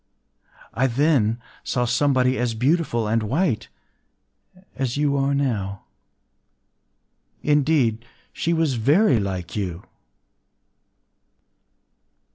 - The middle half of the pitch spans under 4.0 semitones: No, average, 4.8 semitones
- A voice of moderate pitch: No, low, 125 Hz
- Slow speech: Yes, slow, 85 wpm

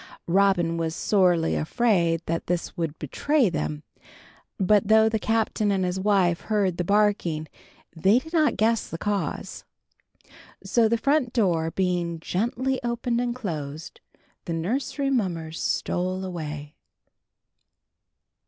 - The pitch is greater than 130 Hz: Yes, high, 190 Hz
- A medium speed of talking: No, slow, 130 wpm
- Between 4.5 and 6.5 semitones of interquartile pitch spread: Yes, average, 5.2 semitones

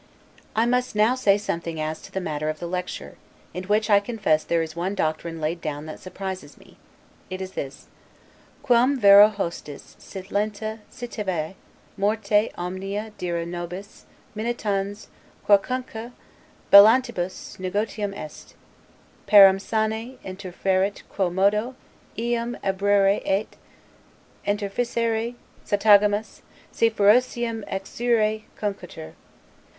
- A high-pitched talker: Yes, high, 200 Hz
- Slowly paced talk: Yes, slow, 115 wpm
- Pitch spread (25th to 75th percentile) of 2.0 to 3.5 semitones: Yes, average, 3.1 semitones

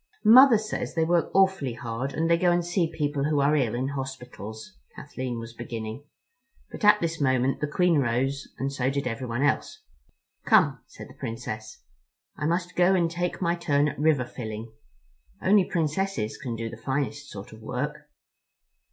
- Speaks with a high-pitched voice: No, medium, 140 Hz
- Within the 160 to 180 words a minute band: Yes, average, 175 wpm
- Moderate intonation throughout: No, wide, 5.7 semitones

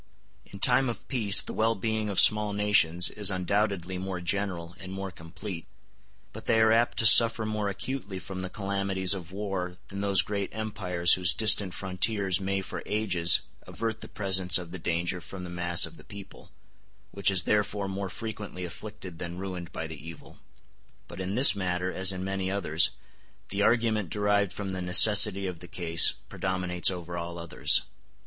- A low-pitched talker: Yes, very low, 95 Hz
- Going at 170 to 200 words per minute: Yes, average, 180 wpm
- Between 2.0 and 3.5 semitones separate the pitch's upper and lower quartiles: Yes, narrow, 2.5 semitones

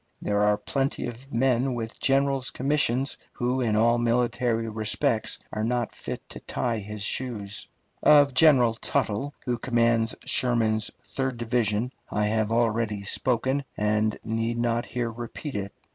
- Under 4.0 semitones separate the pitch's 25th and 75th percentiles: Yes, average, 2.7 semitones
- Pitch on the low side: Yes, low, 120 Hz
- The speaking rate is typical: Yes, average, 145 wpm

